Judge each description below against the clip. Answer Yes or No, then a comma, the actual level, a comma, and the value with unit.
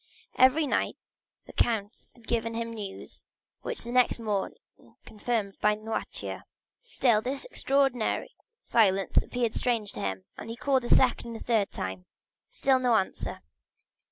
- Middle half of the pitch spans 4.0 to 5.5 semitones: No, average, 3.1 semitones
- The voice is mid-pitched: No, high, 230 Hz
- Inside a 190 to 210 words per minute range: No, average, 150 wpm